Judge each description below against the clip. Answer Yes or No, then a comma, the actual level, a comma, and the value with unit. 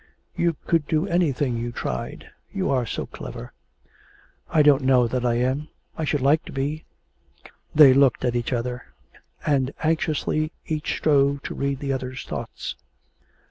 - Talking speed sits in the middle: Yes, average, 155 wpm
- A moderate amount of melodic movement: Yes, average, 3.3 semitones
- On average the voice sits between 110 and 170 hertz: Yes, medium, 140 Hz